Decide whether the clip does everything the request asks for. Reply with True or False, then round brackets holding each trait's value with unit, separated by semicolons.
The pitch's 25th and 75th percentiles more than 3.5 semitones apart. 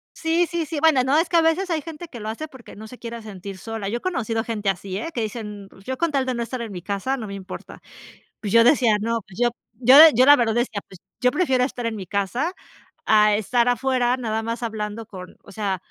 True (4.0 semitones)